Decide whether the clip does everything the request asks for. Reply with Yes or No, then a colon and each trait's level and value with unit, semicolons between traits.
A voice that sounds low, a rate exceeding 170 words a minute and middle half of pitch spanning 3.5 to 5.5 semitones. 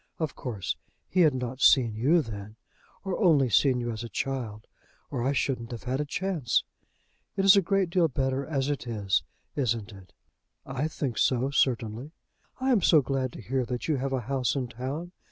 Yes: low, 130 Hz; average, 195 wpm; average, 4.1 semitones